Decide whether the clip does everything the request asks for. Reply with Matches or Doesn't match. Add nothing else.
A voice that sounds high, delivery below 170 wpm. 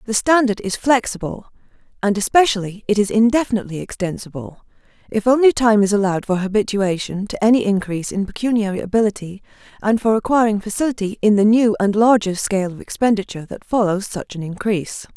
Matches